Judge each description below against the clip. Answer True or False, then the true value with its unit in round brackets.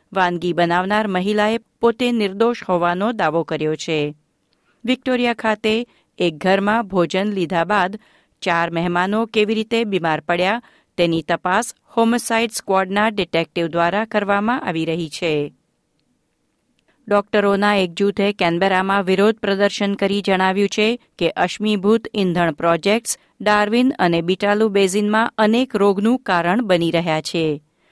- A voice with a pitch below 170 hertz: False (200 Hz)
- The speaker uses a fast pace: False (120 wpm)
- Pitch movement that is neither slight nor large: True (3.8 semitones)